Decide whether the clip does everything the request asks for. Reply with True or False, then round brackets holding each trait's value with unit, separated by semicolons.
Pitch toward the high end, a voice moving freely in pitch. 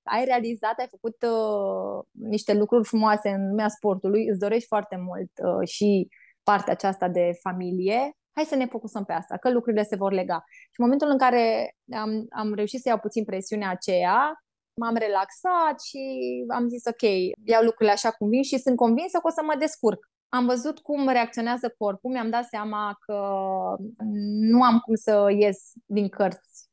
False (220 Hz; 3.2 semitones)